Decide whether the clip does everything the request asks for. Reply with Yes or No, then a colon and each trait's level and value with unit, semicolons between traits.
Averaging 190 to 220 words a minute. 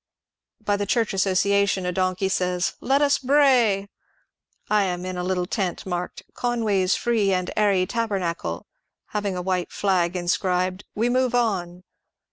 No: average, 170 wpm